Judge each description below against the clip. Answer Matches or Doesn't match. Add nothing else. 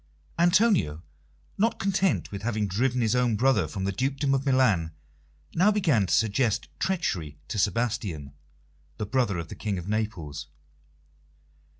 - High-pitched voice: Doesn't match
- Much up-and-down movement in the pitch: Matches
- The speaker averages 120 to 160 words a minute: Matches